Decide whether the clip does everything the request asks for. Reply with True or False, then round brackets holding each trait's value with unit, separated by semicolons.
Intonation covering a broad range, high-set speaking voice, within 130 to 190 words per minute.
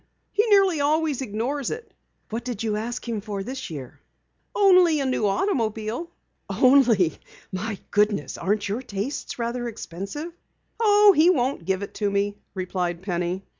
True (6.4 semitones; 230 Hz; 150 wpm)